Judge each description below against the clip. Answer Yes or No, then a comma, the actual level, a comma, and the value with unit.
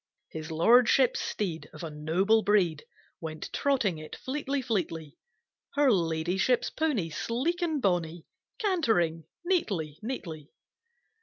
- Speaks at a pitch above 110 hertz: Yes, high, 190 Hz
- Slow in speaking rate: Yes, slow, 110 wpm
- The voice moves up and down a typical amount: No, wide, 8.2 semitones